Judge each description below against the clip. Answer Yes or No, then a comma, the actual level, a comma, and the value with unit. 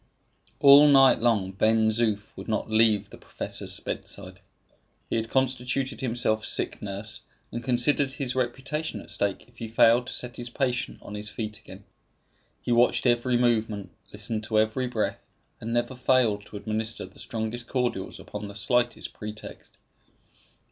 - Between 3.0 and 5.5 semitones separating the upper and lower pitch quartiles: No, narrow, 2.5 semitones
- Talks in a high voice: No, low, 115 Hz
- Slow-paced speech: No, average, 155 wpm